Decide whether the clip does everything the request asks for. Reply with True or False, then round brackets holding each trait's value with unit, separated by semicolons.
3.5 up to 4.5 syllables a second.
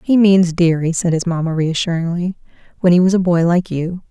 False (5.4 syllables/s)